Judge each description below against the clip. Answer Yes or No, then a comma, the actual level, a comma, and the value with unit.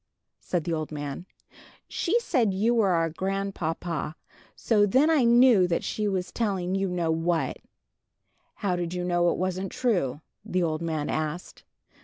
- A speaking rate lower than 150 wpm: No, average, 155 wpm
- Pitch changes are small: No, average, 3.8 semitones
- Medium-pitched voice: Yes, medium, 180 Hz